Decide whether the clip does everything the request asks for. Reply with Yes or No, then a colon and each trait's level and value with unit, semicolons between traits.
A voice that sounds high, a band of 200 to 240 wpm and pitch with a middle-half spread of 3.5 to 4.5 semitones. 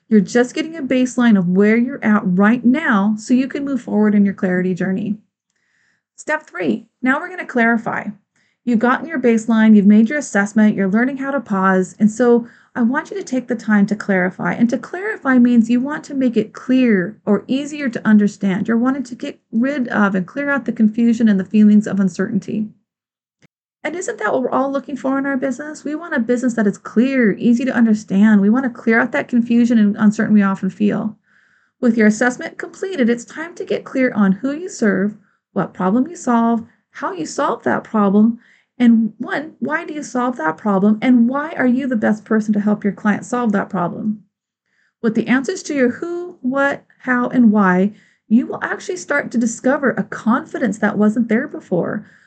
Yes: high, 235 Hz; fast, 205 wpm; average, 4.0 semitones